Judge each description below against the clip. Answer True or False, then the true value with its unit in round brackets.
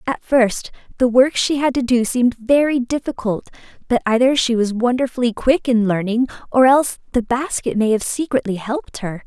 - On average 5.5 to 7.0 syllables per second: False (5.3 syllables/s)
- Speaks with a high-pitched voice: True (245 Hz)